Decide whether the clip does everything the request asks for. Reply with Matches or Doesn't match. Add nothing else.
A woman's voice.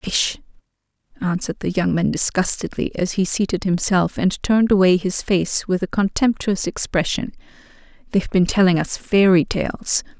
Matches